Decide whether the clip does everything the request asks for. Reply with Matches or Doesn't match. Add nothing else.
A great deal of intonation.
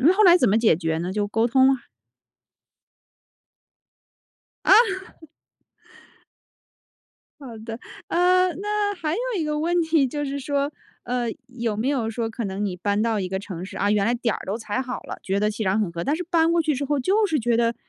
Matches